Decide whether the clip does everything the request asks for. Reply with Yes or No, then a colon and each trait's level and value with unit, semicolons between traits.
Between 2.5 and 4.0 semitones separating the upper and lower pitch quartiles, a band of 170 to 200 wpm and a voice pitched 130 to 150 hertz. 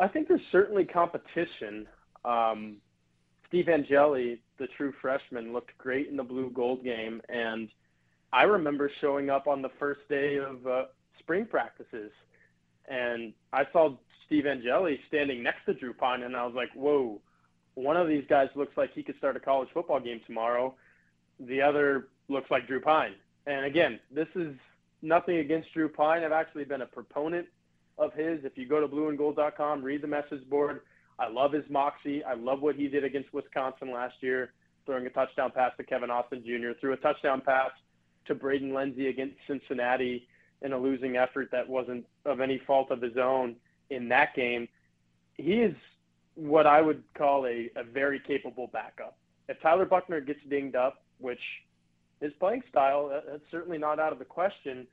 Yes: average, 3.2 semitones; average, 180 wpm; low, 135 Hz